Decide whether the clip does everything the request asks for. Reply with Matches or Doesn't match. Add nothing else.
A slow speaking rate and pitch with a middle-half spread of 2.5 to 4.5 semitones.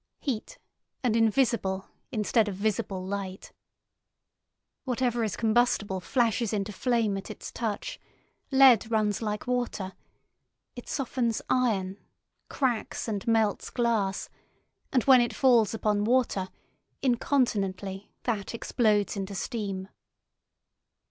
Matches